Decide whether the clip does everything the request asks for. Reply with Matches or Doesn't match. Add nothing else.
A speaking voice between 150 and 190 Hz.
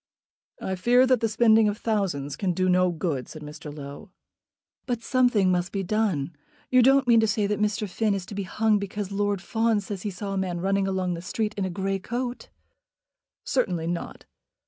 Doesn't match